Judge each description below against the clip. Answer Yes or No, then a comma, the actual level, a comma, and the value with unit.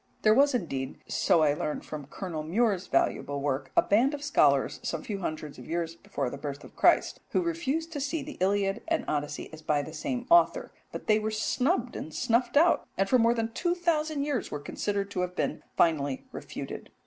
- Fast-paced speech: Yes, fast, 210 wpm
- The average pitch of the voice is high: Yes, high, 200 Hz